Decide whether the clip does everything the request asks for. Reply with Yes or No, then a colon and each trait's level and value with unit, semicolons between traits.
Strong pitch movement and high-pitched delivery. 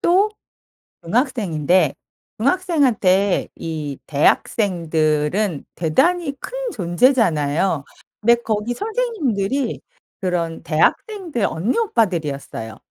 Yes: wide, 8.7 semitones; high, 200 Hz